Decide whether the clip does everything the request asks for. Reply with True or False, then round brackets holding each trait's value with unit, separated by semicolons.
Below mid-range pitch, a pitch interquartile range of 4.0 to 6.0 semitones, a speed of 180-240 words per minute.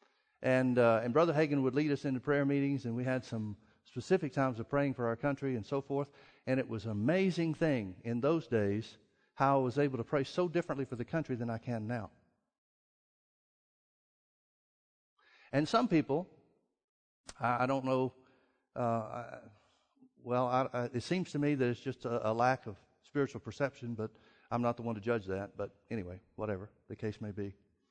False (125 Hz; 3.6 semitones; 190 wpm)